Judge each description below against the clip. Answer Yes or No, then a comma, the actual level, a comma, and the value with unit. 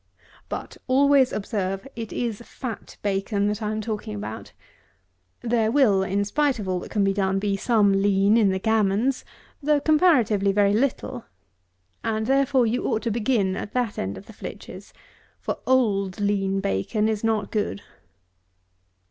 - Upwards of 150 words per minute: Yes, average, 160 wpm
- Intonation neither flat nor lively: Yes, average, 3.5 semitones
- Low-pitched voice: No, high, 210 Hz